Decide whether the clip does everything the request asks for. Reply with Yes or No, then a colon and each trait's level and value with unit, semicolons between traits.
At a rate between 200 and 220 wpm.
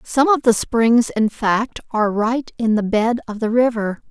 Yes: fast, 205 wpm